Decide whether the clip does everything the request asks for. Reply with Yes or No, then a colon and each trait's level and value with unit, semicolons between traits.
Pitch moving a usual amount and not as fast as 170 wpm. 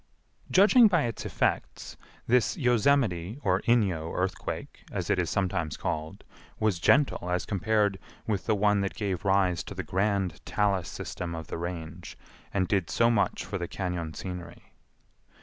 Yes: average, 3.7 semitones; average, 155 wpm